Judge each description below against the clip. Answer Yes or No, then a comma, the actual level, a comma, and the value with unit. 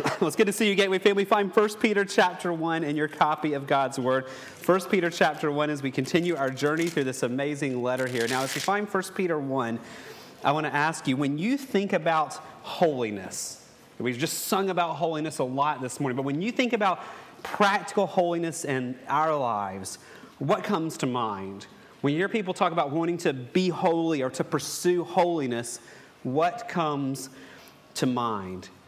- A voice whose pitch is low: No, medium, 155 Hz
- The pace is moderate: Yes, average, 195 wpm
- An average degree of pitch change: No, wide, 5.7 semitones